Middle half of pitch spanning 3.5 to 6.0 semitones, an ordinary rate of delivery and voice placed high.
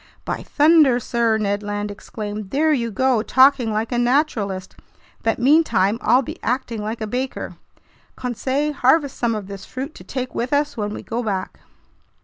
Yes: average, 3.9 semitones; average, 170 wpm; high, 240 Hz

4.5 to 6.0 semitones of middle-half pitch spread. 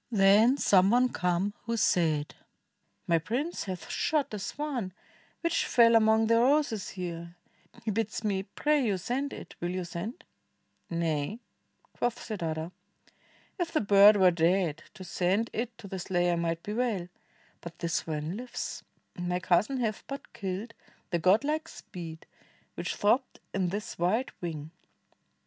Yes: average, 5.1 semitones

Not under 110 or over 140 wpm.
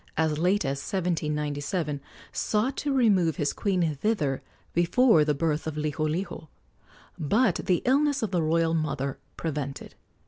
Yes: slow, 135 wpm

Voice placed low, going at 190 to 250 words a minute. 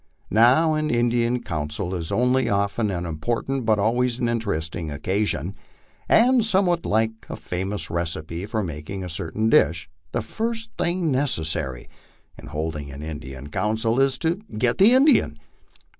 No: low, 110 Hz; average, 155 wpm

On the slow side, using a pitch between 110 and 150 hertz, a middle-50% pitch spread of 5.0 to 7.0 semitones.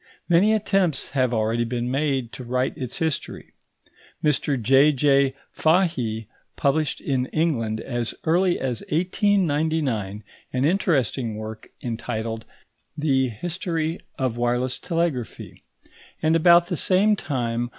Yes: slow, 120 wpm; low, 135 Hz; wide, 5.4 semitones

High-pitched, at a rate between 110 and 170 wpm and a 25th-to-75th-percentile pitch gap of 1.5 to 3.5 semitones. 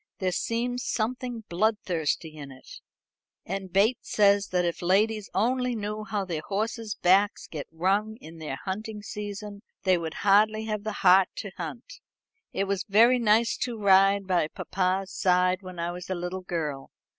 Yes: high, 195 Hz; average, 165 wpm; average, 3.2 semitones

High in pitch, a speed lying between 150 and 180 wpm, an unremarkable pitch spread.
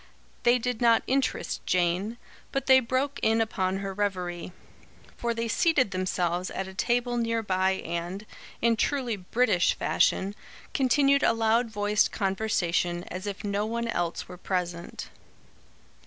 No: high, 210 Hz; average, 140 wpm; average, 4.3 semitones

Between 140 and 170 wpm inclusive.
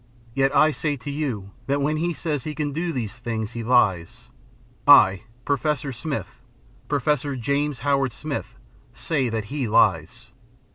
Yes: average, 150 wpm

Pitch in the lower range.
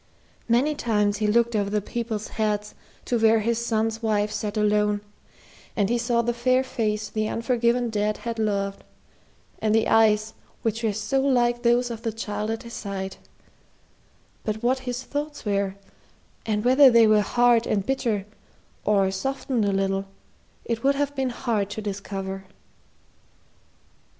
No: high, 220 Hz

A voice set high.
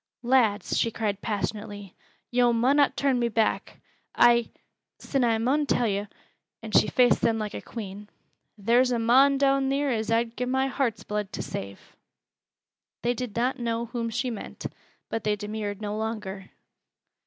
Yes: high, 230 Hz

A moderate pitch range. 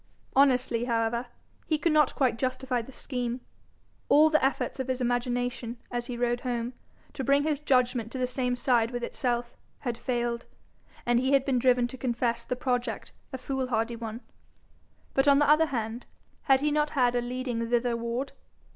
No: narrow, 1.9 semitones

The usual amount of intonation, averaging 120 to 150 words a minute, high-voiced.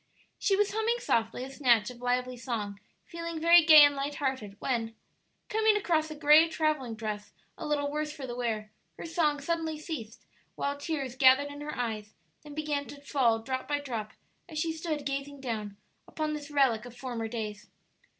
No: average, 4.5 semitones; average, 185 wpm; very high, 280 Hz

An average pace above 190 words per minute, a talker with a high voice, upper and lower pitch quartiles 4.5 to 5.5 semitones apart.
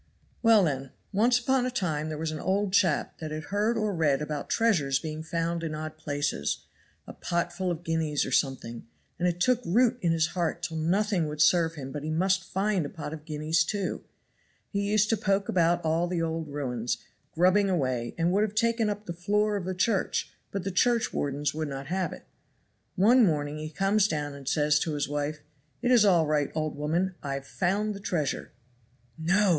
No: fast, 205 wpm; medium, 165 Hz; average, 4.8 semitones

